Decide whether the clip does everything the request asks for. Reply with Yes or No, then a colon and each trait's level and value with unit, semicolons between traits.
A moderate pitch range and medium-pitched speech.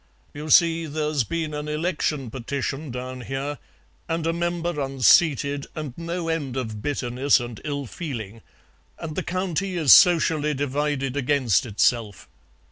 Yes: average, 4.1 semitones; medium, 145 Hz